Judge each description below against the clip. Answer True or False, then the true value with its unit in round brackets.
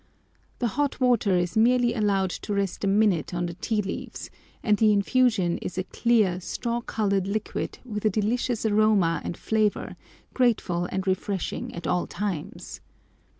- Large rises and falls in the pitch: False (3.2 semitones)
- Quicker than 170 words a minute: False (155 wpm)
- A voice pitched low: False (205 Hz)